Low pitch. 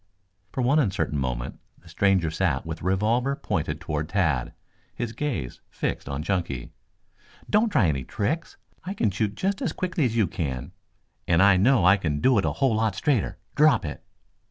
Yes: low, 100 Hz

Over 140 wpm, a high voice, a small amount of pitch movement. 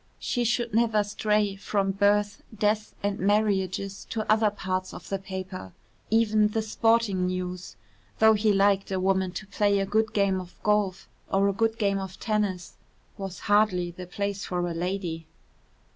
Yes: average, 165 wpm; high, 200 Hz; narrow, 2.1 semitones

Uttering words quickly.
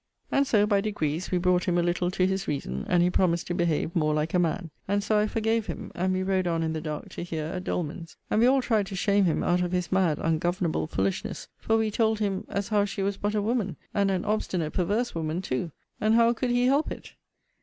Yes: fast, 250 wpm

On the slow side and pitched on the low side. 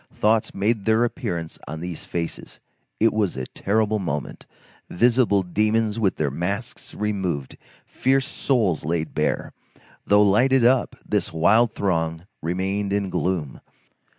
Yes: slow, 130 wpm; low, 100 Hz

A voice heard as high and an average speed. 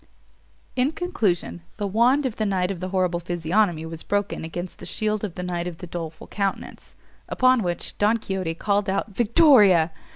Yes: high, 195 Hz; average, 175 wpm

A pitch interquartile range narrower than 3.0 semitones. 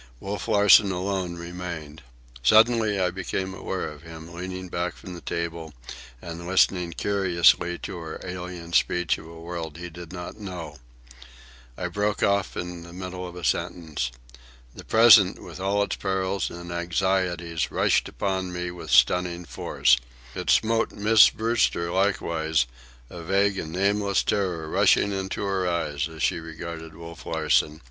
Yes: narrow, 2.4 semitones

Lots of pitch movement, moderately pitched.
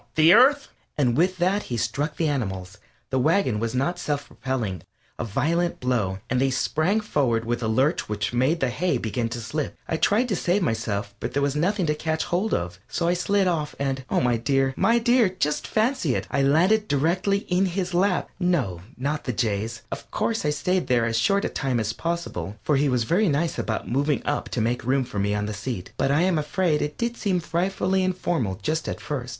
Yes: wide, 7.0 semitones; medium, 145 Hz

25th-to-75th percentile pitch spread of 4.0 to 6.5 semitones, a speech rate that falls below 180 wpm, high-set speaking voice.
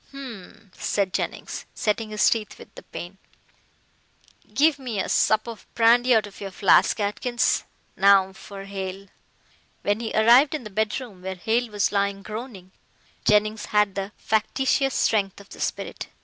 No: average, 2.9 semitones; average, 155 wpm; high, 210 Hz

